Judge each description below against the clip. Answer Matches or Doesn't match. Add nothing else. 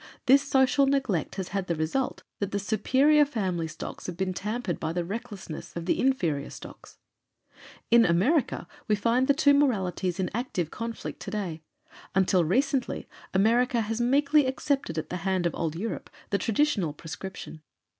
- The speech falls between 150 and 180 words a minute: Matches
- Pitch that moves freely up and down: Matches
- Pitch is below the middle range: Doesn't match